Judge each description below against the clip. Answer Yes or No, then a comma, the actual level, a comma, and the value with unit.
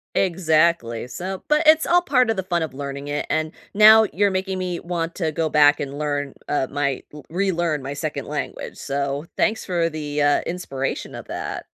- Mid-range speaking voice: Yes, medium, 160 Hz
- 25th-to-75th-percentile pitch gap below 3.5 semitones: No, average, 4.5 semitones